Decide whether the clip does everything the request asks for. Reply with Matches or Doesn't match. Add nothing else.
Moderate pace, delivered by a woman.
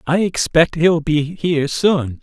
Doesn't match